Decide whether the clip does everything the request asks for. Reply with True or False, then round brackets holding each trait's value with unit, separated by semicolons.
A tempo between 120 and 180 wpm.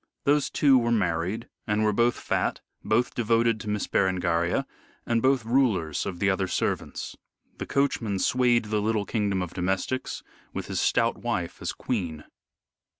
True (155 wpm)